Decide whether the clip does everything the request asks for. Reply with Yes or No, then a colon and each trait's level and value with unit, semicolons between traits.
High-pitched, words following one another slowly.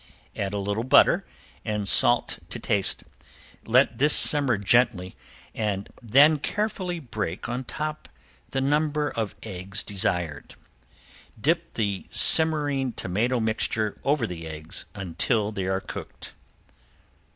No: low, 110 Hz; slow, 120 wpm